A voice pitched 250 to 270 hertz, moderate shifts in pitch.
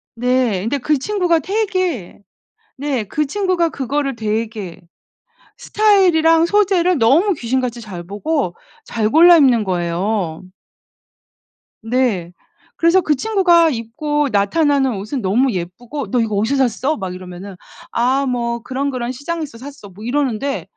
No: very high, 260 Hz; wide, 6.6 semitones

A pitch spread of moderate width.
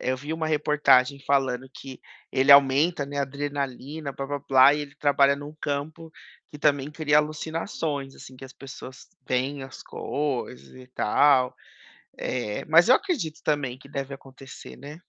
No: narrow, 2.0 semitones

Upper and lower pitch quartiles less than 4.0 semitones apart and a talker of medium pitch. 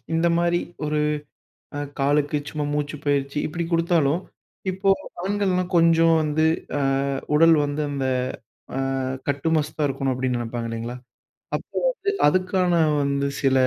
Yes: average, 3.5 semitones; medium, 150 Hz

